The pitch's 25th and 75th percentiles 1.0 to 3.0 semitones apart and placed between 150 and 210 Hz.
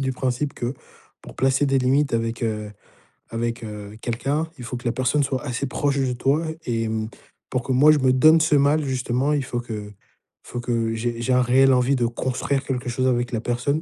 No: narrow, 2.5 semitones; low, 125 Hz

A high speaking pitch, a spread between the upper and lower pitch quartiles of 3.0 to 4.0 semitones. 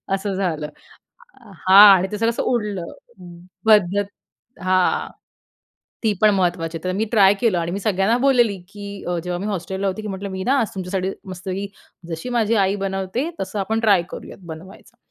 No: high, 195 Hz; narrow, 2.4 semitones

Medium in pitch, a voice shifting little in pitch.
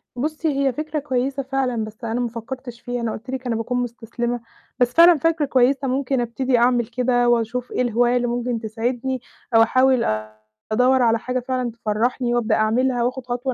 No: high, 245 Hz; narrow, 1.8 semitones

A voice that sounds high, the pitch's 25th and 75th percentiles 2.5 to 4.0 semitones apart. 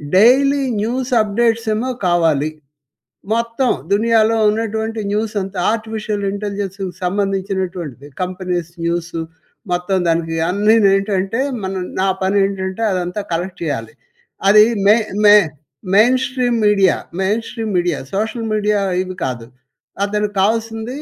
Yes: high, 205 Hz; average, 3.2 semitones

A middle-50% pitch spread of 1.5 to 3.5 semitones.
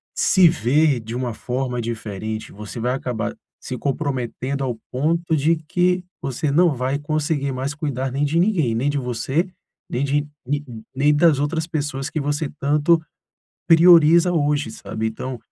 No: average, 4.0 semitones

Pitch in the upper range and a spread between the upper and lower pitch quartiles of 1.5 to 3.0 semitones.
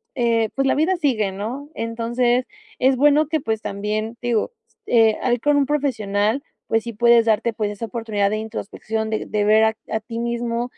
Yes: high, 230 Hz; narrow, 2.5 semitones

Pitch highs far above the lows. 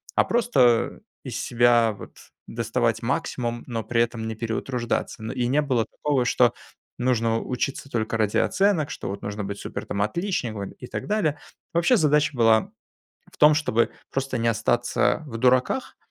No: average, 3.9 semitones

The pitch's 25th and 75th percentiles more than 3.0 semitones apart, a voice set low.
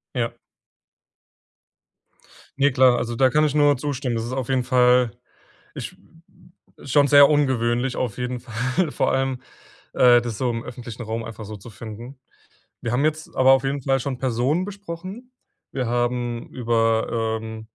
No: average, 2.7 semitones; low, 125 Hz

